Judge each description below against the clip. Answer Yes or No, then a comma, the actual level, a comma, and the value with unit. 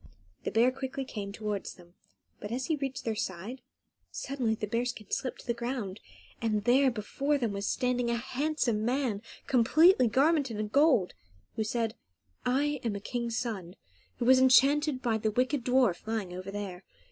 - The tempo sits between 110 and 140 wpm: No, average, 175 wpm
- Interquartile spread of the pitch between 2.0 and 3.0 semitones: No, average, 3.8 semitones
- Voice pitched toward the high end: Yes, high, 235 Hz